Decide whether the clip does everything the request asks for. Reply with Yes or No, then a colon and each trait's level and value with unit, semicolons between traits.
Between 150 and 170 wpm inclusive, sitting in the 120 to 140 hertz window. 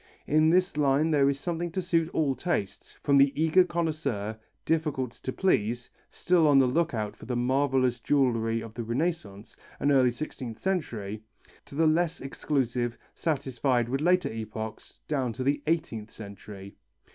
Yes: average, 160 wpm; low, 135 Hz